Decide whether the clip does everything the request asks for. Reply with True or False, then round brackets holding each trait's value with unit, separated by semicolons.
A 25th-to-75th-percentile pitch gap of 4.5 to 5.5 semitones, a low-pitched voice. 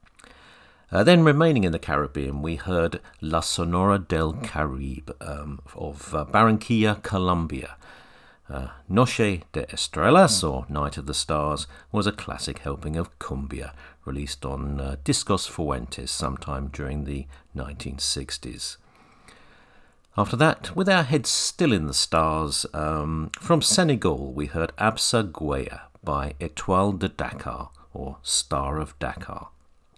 True (5.0 semitones; 75 Hz)